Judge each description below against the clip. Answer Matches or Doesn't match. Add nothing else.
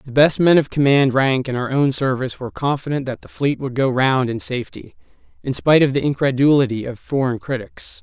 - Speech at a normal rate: Doesn't match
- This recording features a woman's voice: Doesn't match